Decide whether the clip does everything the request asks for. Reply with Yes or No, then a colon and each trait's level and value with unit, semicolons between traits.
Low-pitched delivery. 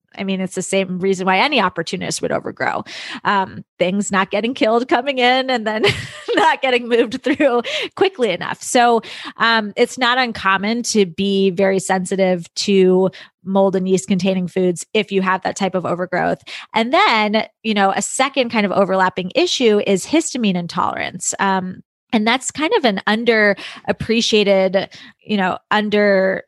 No: high, 200 Hz